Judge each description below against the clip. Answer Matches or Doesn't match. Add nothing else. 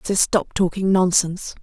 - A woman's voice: Matches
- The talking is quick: Doesn't match